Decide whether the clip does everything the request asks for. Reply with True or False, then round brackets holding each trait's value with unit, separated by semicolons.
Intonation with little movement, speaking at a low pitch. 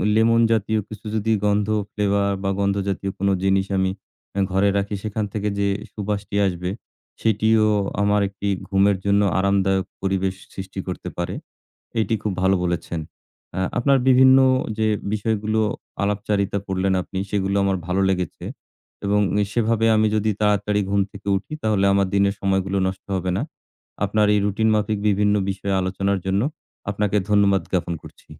True (1.5 semitones; 100 Hz)